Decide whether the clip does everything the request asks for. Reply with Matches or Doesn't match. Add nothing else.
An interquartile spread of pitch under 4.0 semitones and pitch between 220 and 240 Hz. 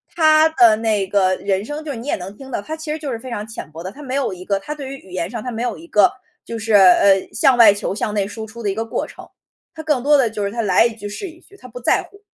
Doesn't match